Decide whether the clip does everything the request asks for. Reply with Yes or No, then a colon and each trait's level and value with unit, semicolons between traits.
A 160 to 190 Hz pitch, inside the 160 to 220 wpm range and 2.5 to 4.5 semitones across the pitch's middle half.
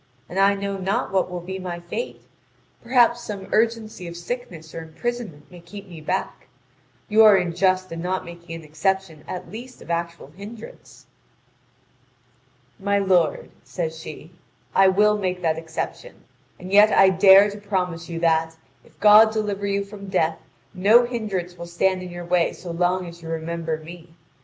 Yes: medium, 185 Hz; average, 170 wpm; average, 3.1 semitones